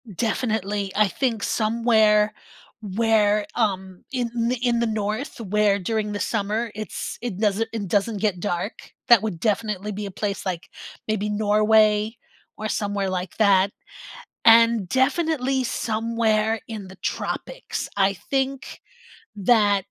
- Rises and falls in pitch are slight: Yes, narrow, 2.1 semitones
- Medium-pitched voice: No, high, 215 Hz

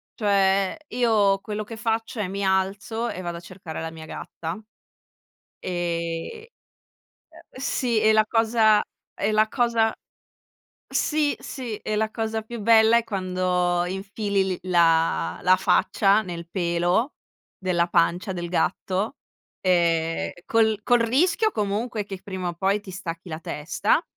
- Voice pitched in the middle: No, high, 200 Hz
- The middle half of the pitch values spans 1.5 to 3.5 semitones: No, average, 3.9 semitones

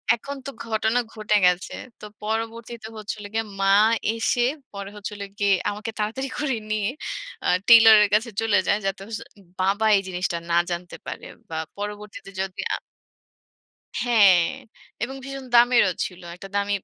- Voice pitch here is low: No, high, 210 Hz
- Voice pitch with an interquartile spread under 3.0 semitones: Yes, narrow, 2.5 semitones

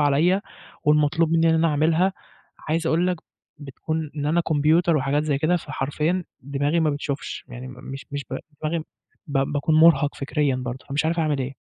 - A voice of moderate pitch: Yes, medium, 150 Hz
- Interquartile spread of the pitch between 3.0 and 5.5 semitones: No, narrow, 2.6 semitones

